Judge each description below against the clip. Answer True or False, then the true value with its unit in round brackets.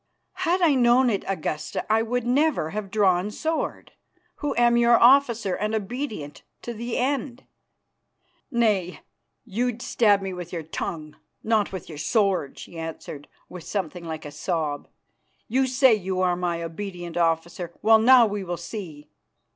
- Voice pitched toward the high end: True (205 Hz)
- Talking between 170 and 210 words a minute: False (155 wpm)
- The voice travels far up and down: True (5.7 semitones)